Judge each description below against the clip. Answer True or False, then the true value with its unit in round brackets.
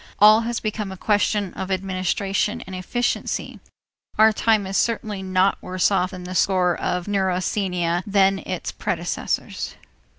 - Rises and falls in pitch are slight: True (2.2 semitones)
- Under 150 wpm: True (140 wpm)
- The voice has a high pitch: True (195 Hz)